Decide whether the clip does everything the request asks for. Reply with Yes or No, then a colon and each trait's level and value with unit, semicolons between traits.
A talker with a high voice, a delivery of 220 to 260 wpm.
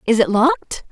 No: high, 245 Hz; average, 200 wpm